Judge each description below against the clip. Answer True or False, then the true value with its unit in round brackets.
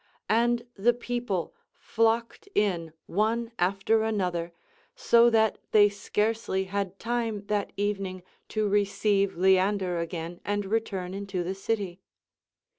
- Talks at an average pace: False (120 wpm)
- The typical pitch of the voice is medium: False (200 Hz)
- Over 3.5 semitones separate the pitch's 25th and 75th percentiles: False (2.9 semitones)